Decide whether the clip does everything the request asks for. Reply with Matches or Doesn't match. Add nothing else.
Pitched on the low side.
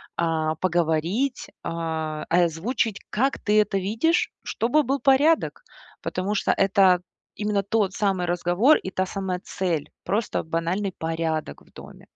Doesn't match